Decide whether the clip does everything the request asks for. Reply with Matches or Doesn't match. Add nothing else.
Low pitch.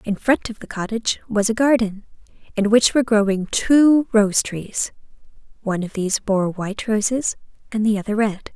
Doesn't match